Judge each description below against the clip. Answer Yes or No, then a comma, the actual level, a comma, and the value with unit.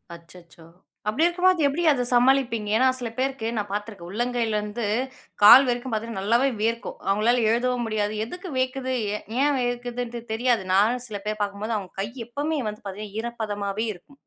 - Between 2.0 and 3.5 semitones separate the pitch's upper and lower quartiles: Yes, average, 3.2 semitones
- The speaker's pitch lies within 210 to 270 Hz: Yes, high, 230 Hz